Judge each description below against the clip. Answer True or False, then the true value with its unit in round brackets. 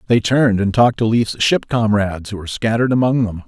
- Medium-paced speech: False (225 wpm)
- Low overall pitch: True (110 Hz)